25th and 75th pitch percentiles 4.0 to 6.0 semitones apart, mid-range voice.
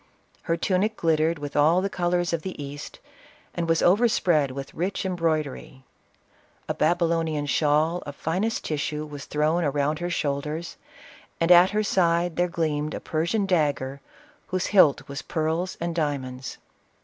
No: average, 3.1 semitones; medium, 165 Hz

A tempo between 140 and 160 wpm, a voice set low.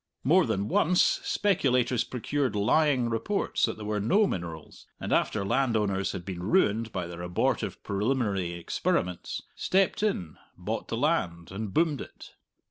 Yes: average, 145 wpm; low, 110 Hz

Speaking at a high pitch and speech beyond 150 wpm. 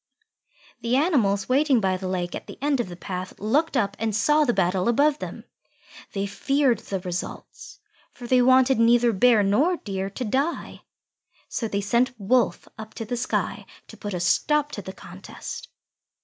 Yes: high, 230 Hz; average, 175 wpm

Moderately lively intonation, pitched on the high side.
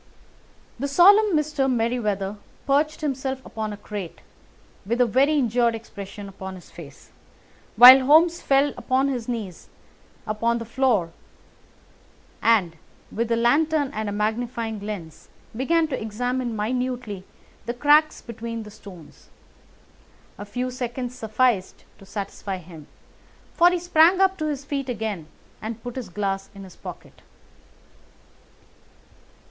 Yes: average, 4.5 semitones; high, 235 Hz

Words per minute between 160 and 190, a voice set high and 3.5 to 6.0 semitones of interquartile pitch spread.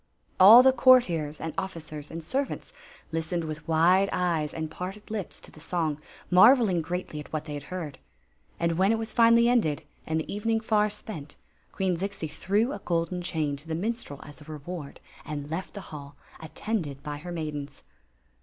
No: average, 180 wpm; medium, 170 Hz; average, 4.7 semitones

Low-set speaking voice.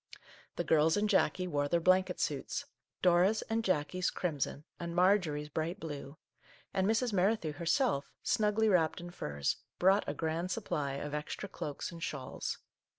No: medium, 175 Hz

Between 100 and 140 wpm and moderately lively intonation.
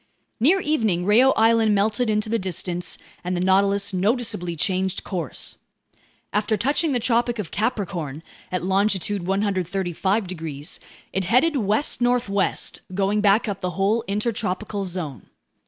Yes: slow, 135 wpm; average, 3.4 semitones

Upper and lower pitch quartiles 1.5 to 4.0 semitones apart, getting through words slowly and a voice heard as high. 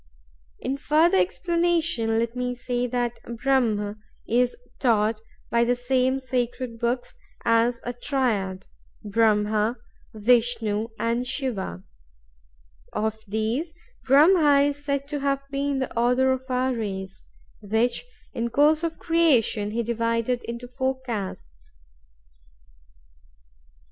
Yes: average, 3.2 semitones; slow, 110 wpm; high, 245 Hz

